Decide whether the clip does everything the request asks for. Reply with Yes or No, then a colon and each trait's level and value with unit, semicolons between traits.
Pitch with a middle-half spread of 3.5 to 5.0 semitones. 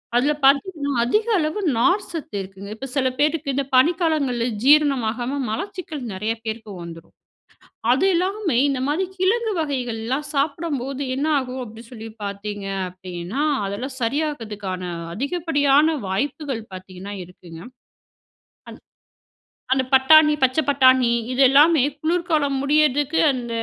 No: wide, 5.4 semitones